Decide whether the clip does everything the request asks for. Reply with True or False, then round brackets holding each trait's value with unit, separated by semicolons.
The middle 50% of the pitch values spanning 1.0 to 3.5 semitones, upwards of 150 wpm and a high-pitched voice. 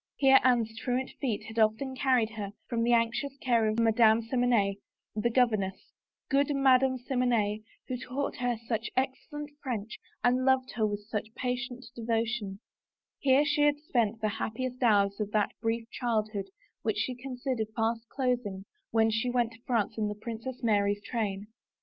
True (2.8 semitones; 175 wpm; 235 Hz)